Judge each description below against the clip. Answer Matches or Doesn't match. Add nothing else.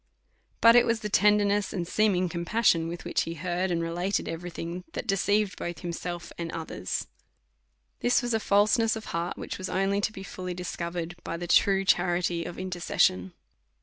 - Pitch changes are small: Doesn't match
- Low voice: Doesn't match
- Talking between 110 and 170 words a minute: Doesn't match